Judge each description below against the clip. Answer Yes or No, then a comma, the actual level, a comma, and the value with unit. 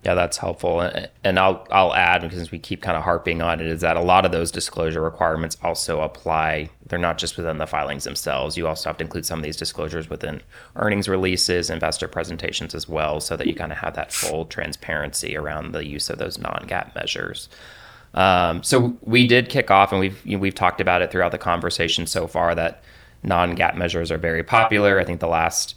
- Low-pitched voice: Yes, very low, 85 Hz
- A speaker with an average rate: No, fast, 215 wpm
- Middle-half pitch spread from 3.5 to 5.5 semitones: No, narrow, 2.5 semitones